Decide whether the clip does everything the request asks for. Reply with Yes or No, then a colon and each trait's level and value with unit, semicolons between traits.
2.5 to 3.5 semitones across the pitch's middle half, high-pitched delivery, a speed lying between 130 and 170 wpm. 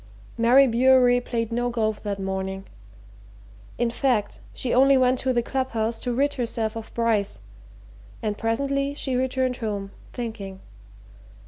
Yes: average, 3.0 semitones; high, 235 Hz; average, 145 wpm